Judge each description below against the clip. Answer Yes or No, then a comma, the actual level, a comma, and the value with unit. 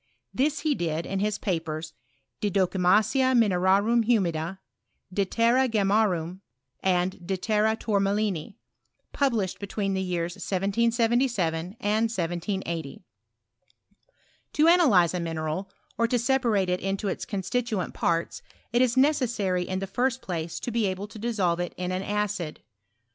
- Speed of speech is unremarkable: Yes, average, 145 wpm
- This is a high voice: Yes, high, 195 Hz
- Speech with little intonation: No, average, 4.4 semitones